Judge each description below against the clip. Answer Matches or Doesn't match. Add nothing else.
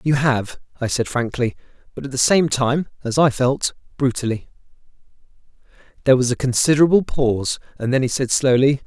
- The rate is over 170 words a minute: Doesn't match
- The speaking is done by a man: Matches